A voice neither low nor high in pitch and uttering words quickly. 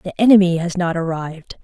No: medium, 175 Hz; average, 185 wpm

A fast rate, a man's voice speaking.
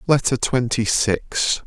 No: slow, 110 wpm; male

